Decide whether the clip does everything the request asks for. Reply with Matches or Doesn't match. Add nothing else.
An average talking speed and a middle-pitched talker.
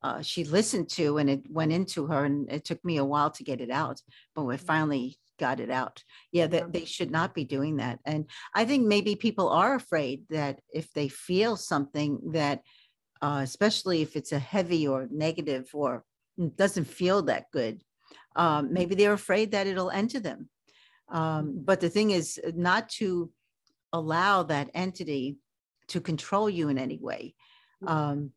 Matches